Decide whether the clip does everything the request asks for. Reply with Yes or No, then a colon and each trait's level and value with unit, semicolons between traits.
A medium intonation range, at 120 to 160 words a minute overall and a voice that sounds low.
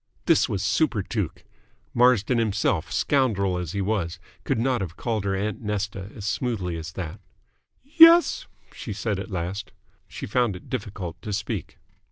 Yes: average, 3.9 semitones; average, 155 wpm; low, 100 Hz